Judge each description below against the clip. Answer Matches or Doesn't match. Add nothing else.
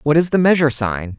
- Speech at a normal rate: Doesn't match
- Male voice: Matches